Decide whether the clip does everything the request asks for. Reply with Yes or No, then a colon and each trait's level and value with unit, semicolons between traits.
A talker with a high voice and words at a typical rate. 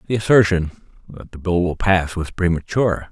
No: very low, 90 Hz; average, 175 wpm